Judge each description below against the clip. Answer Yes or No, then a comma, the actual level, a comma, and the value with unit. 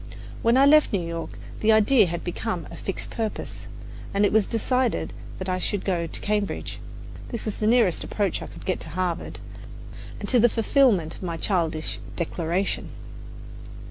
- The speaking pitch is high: Yes, high, 200 Hz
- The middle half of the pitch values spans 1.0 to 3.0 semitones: No, average, 4.5 semitones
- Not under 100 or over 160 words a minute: No, average, 175 wpm